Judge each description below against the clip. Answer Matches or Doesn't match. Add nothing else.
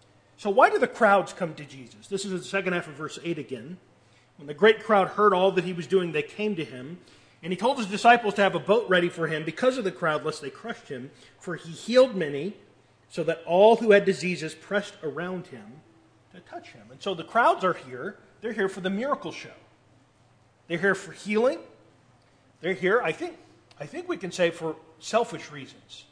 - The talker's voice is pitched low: Doesn't match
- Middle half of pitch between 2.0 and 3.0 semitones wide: Doesn't match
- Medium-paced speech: Doesn't match